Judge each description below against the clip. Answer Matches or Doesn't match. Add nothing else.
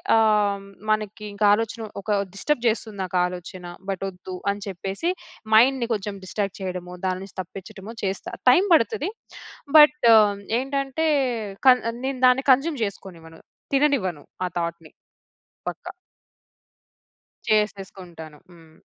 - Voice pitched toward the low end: Doesn't match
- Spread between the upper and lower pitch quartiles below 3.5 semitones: Doesn't match